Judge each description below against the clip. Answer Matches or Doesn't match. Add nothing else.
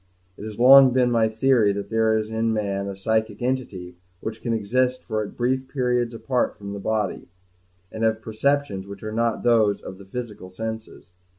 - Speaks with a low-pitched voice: Matches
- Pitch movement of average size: Matches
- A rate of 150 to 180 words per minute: Doesn't match